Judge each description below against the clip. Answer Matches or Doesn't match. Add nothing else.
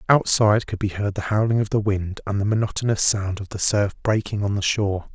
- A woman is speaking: Doesn't match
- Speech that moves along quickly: Matches